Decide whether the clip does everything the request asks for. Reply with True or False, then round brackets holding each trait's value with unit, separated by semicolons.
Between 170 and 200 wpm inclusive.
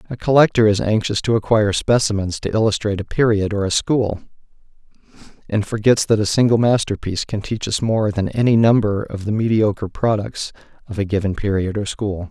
True (180 wpm)